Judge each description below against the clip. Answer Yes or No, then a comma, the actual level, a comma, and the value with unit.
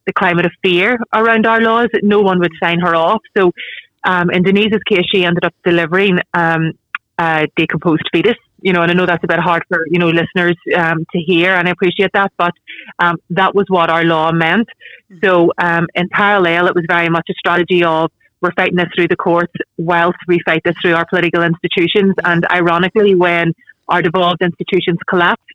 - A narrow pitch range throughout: Yes, narrow, 1.8 semitones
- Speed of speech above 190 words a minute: Yes, fast, 205 wpm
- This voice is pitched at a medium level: Yes, medium, 175 Hz